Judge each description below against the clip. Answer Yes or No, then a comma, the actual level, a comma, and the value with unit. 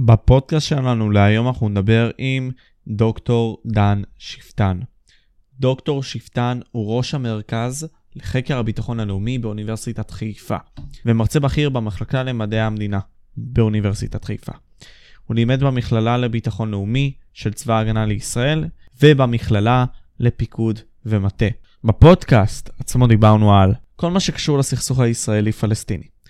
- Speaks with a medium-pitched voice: No, low, 115 Hz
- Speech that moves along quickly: No, average, 105 wpm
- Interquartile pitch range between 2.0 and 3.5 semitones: Yes, average, 3.1 semitones